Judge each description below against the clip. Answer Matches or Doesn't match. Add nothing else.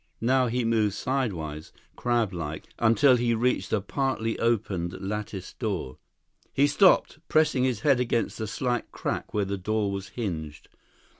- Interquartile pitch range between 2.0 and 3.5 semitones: Doesn't match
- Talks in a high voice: Doesn't match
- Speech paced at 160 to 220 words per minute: Doesn't match